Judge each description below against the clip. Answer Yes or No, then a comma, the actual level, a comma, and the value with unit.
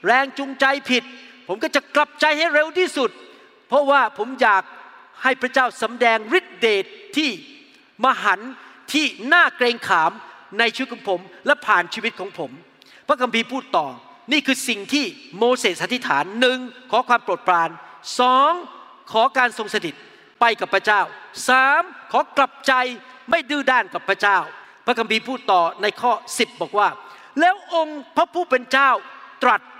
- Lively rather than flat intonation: No, average, 4.3 semitones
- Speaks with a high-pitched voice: Yes, very high, 260 Hz